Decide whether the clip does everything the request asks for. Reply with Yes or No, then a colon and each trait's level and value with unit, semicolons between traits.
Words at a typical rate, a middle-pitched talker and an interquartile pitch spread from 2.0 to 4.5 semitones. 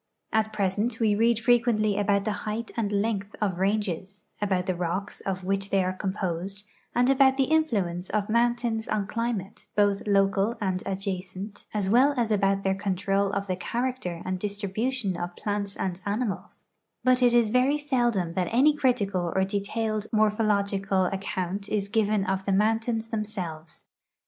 No: average, 160 wpm; high, 205 Hz; average, 2.8 semitones